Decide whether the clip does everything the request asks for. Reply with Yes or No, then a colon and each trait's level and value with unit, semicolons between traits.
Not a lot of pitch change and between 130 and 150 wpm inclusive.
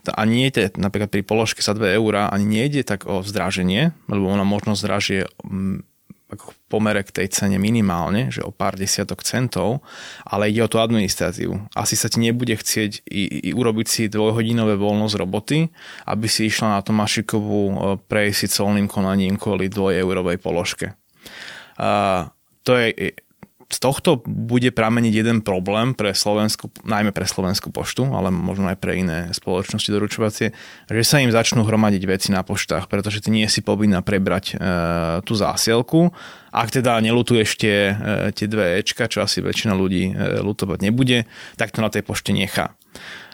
No: narrow, 2.3 semitones; fast, 165 wpm